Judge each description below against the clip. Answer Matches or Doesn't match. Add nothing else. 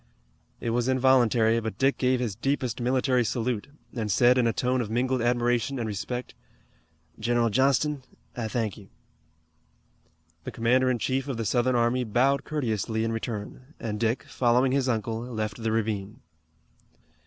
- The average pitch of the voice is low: Matches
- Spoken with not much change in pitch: Matches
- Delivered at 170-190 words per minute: Doesn't match